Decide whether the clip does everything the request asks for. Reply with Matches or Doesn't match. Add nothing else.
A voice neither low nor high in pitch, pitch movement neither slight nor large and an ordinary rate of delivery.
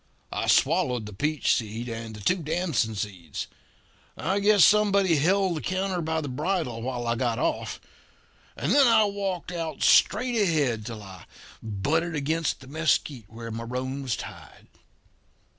Doesn't match